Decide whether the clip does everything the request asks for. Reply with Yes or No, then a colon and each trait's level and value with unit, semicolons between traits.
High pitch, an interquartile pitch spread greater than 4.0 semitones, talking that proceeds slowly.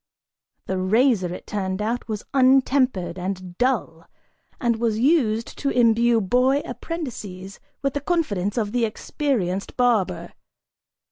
Yes: high, 225 Hz; average, 5.2 semitones; slow, 125 wpm